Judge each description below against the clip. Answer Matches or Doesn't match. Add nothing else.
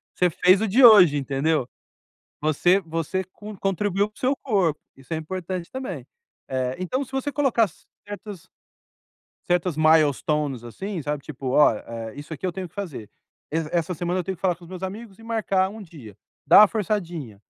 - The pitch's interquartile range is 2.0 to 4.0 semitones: Doesn't match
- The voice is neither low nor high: Matches